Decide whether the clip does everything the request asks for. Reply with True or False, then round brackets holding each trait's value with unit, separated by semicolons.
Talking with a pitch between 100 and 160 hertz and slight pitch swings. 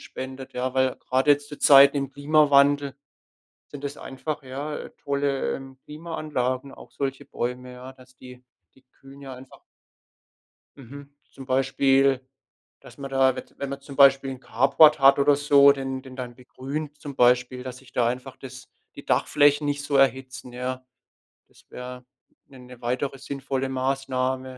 True (135 Hz; 1.6 semitones)